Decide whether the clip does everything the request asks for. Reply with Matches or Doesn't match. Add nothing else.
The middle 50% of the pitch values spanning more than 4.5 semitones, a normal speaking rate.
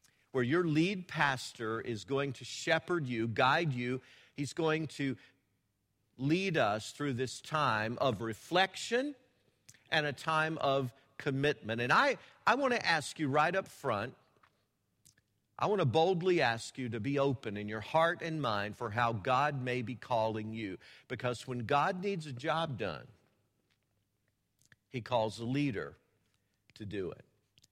Matches